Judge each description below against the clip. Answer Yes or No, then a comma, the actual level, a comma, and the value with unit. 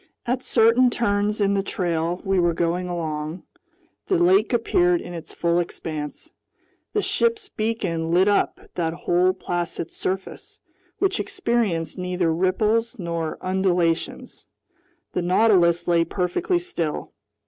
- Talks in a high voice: No, medium, 180 Hz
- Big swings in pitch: No, average, 4.7 semitones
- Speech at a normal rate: No, slow, 125 wpm